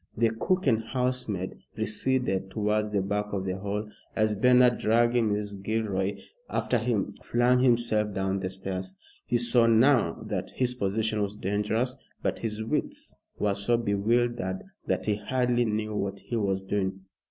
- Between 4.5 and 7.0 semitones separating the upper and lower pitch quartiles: No, average, 3.2 semitones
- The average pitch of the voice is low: Yes, low, 105 Hz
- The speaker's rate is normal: Yes, average, 155 wpm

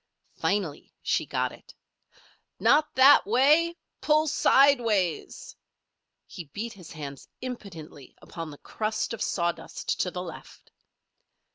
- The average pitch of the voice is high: Yes, high, 205 Hz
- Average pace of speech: No, slow, 115 wpm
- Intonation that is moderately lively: No, wide, 7.7 semitones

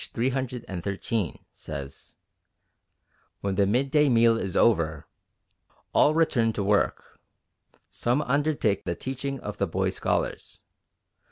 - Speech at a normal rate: No, slow, 105 wpm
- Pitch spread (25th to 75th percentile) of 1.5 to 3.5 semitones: No, average, 5.2 semitones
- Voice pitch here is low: Yes, low, 115 Hz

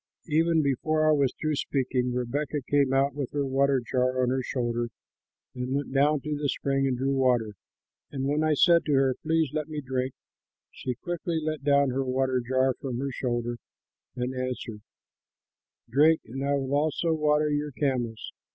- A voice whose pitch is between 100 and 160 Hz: Yes, low, 135 Hz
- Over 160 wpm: Yes, average, 180 wpm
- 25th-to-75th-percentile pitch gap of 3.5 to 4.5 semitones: No, narrow, 2.6 semitones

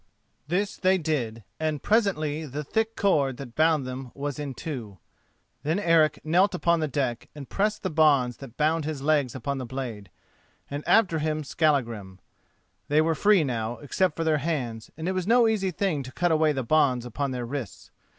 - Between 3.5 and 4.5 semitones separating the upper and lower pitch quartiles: Yes, average, 4.2 semitones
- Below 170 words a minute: No, average, 190 wpm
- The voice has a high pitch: No, medium, 150 Hz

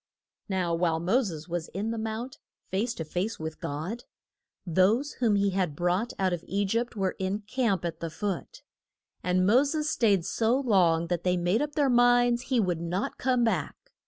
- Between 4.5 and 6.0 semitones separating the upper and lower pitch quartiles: Yes, average, 5.2 semitones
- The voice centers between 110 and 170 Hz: No, high, 195 Hz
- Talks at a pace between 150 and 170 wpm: No, average, 195 wpm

